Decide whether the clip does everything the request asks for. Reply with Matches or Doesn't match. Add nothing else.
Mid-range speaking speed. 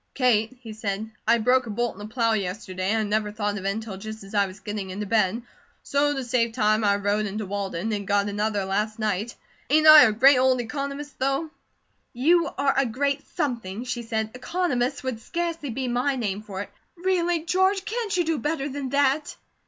Doesn't match